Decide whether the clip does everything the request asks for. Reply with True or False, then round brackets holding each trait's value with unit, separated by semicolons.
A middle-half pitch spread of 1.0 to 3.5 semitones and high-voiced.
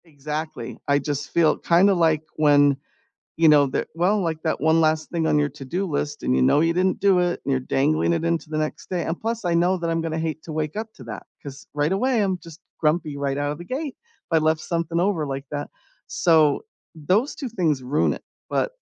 False (3.2 semitones; 160 Hz)